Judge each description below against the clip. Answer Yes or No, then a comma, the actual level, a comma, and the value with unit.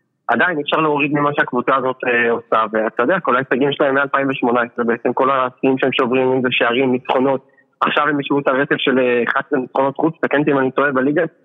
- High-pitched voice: No, low, 135 Hz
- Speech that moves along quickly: Yes, fast, 195 wpm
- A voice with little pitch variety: Yes, narrow, 2.2 semitones